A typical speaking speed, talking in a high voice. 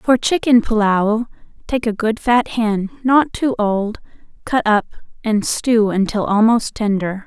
Yes: average, 150 wpm; high, 225 Hz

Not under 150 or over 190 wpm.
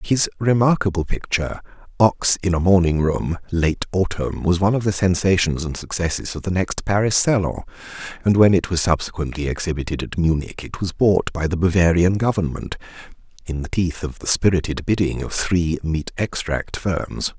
Yes: average, 170 wpm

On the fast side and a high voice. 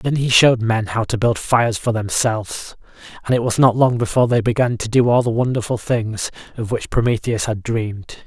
No: fast, 210 wpm; low, 115 Hz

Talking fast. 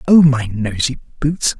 No: average, 150 wpm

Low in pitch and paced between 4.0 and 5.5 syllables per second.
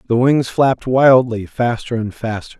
Yes: low, 120 Hz; 4.6 syllables/s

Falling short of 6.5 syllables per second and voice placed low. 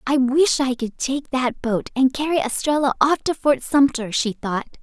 No: 4.5 syllables/s; very high, 265 Hz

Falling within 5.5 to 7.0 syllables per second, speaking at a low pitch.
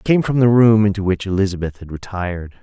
Yes: 6.2 syllables/s; low, 100 Hz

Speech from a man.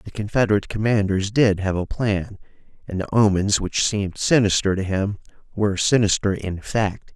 Yes: male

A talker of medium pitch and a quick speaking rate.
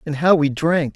Yes: medium, 155 Hz; fast, 250 wpm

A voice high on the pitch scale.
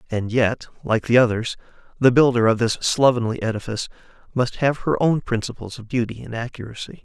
No: low, 120 Hz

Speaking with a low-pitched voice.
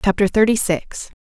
No: high, 200 Hz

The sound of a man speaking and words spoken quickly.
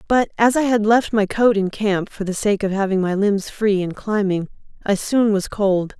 No: female; fast, 230 wpm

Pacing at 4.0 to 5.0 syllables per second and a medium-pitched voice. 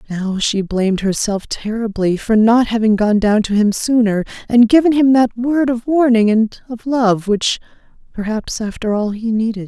No: 4.6 syllables/s; high, 220 Hz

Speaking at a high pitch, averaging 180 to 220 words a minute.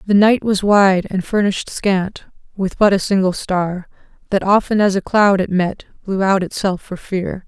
Yes: high, 195 Hz; average, 195 wpm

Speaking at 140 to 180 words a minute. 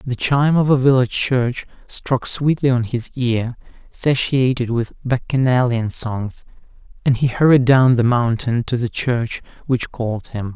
Yes: average, 155 wpm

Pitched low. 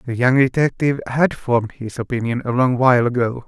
Yes: low, 125 Hz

